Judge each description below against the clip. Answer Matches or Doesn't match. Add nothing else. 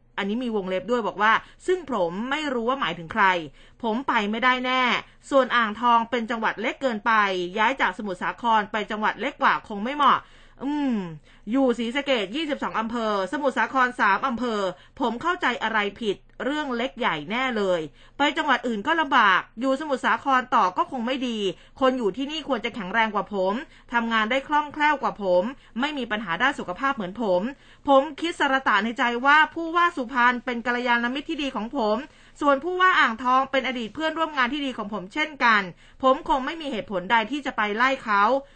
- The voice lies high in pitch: Matches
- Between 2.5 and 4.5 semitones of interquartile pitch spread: Matches